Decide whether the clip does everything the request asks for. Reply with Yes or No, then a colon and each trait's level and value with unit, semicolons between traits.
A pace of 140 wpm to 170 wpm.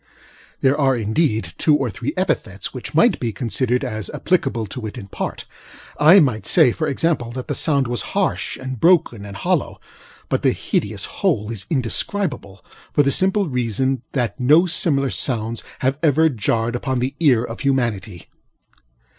Yes: average, 165 wpm